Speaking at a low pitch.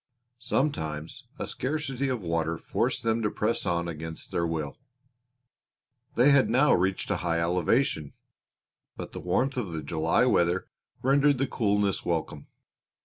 Yes: very low, 95 Hz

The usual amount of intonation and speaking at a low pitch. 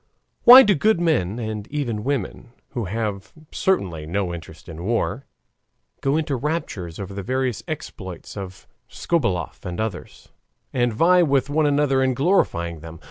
No: wide, 7.8 semitones; low, 120 Hz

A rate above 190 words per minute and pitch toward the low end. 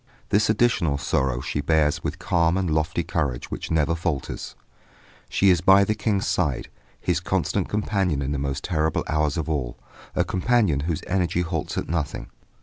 No: average, 170 wpm; very low, 80 Hz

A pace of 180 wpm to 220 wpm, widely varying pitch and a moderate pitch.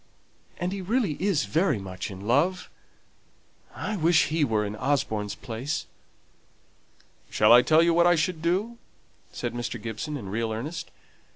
No: average, 155 wpm; wide, 7.9 semitones; medium, 150 Hz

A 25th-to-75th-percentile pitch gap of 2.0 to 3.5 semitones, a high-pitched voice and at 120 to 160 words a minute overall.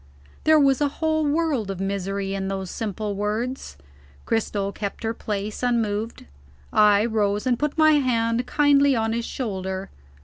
No: average, 4.7 semitones; high, 225 Hz; average, 150 wpm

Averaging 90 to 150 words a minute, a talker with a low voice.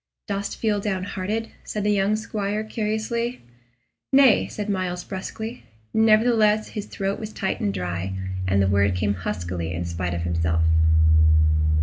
No: average, 140 wpm; high, 200 Hz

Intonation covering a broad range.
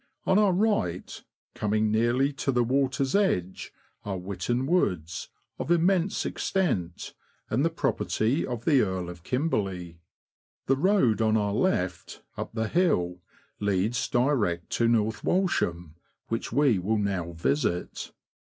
Yes: wide, 7.4 semitones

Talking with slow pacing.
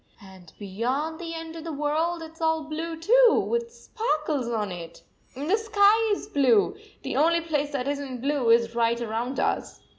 No: average, 200 wpm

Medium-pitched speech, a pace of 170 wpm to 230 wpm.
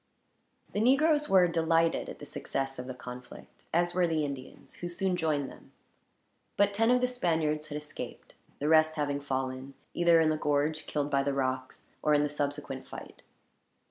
Yes: medium, 155 Hz; average, 180 wpm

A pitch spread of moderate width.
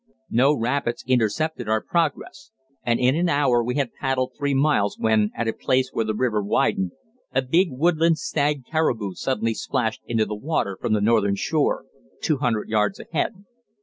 Yes: average, 4.8 semitones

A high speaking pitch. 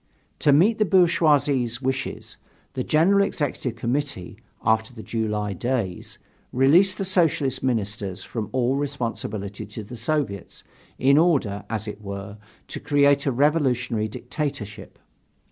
No: low, 130 Hz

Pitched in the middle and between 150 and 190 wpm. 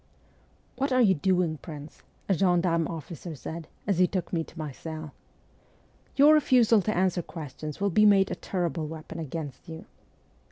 Yes: medium, 170 Hz; average, 175 wpm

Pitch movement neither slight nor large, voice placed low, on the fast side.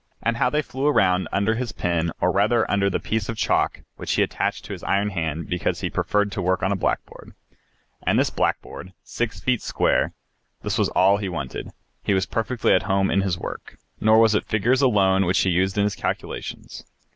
Yes: average, 3.0 semitones; low, 100 Hz; fast, 210 wpm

